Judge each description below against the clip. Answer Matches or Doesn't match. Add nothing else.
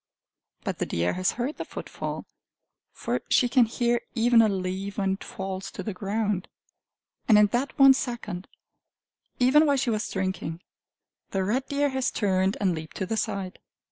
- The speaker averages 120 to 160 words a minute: Doesn't match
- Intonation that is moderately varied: Matches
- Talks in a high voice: Matches